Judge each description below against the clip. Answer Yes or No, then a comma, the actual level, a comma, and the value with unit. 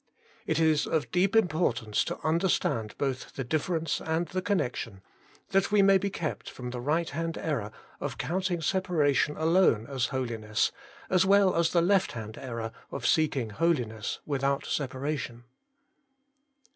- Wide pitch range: Yes, wide, 6.1 semitones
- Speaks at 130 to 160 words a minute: Yes, average, 150 wpm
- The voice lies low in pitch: No, medium, 155 Hz